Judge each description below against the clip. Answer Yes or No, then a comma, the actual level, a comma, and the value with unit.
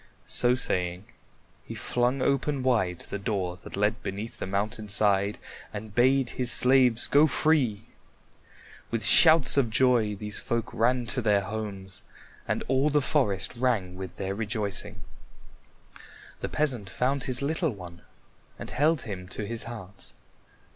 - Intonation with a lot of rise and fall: No, average, 4.5 semitones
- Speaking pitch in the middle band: No, low, 110 Hz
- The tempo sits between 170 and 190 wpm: No, average, 145 wpm